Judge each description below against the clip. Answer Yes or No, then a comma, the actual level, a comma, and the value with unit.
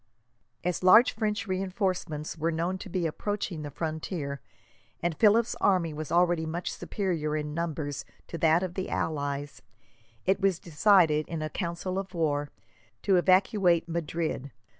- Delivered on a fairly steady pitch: No, average, 3.3 semitones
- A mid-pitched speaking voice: Yes, medium, 170 Hz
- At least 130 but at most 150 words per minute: Yes, average, 145 wpm